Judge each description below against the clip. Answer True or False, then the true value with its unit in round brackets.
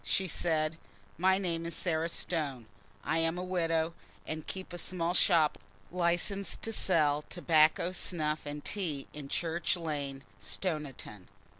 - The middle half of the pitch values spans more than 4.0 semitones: False (2.7 semitones)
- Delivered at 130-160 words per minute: True (140 wpm)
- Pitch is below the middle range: False (165 Hz)